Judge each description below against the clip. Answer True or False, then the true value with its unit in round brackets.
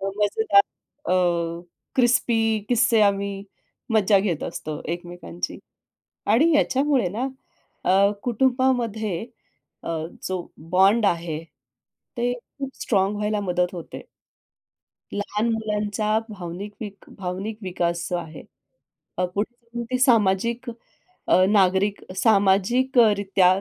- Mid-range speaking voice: False (205 Hz)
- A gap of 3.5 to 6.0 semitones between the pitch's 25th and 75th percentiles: True (3.8 semitones)